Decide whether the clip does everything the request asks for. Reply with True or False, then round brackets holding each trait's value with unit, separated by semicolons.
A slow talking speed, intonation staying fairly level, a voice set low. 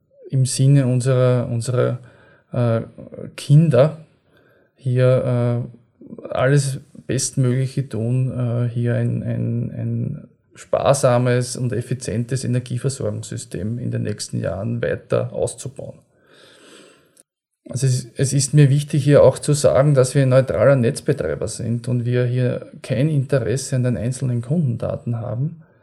True (120 wpm; 2.3 semitones; 125 Hz)